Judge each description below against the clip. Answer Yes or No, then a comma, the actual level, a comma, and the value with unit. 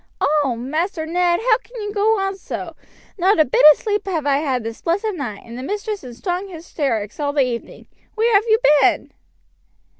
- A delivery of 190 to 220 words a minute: Yes, average, 200 wpm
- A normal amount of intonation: No, wide, 7.0 semitones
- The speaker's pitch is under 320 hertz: No, very high, 335 Hz